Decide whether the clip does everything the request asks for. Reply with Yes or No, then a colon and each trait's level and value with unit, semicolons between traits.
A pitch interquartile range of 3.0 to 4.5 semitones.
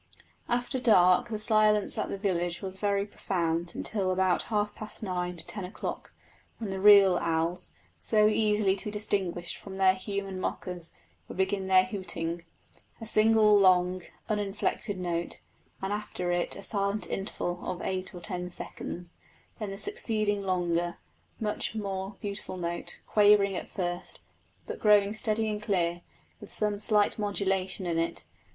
No: narrow, 2.6 semitones